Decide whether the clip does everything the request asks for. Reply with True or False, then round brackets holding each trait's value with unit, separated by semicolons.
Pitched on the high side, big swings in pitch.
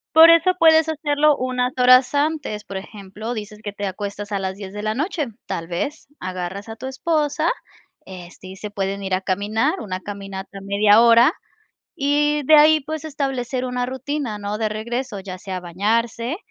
True (225 Hz; 6.3 semitones)